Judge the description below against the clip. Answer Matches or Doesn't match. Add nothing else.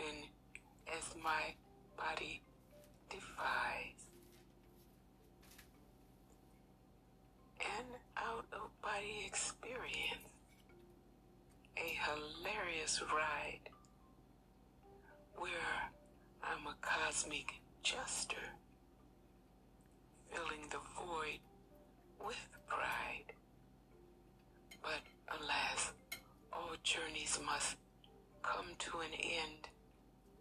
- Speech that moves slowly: Matches